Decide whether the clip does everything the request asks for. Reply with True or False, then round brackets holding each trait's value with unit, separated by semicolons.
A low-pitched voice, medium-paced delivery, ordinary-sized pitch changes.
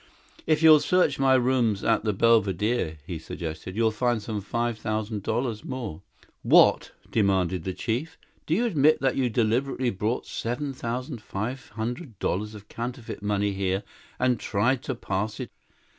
True (115 Hz; 160 wpm; 3.8 semitones)